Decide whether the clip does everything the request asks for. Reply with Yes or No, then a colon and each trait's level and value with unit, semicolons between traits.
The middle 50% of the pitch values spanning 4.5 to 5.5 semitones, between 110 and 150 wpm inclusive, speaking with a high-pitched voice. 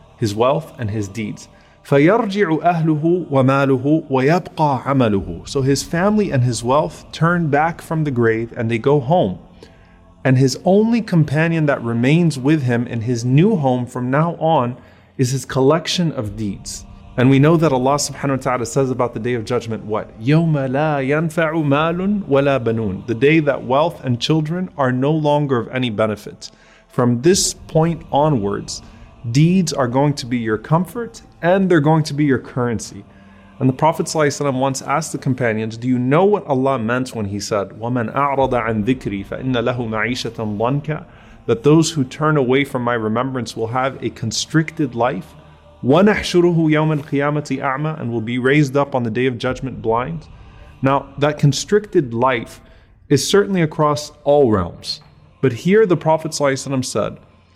No: average, 4.8 semitones; average, 145 wpm; low, 135 Hz